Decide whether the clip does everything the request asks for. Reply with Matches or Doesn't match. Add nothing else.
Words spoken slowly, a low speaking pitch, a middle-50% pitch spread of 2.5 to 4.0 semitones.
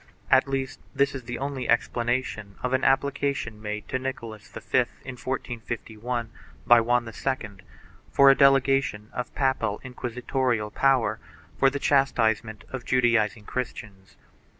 Matches